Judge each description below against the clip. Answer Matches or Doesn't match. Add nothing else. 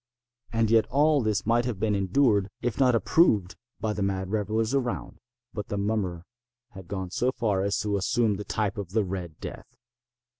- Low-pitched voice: Matches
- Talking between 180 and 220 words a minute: Matches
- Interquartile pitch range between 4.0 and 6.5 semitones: Doesn't match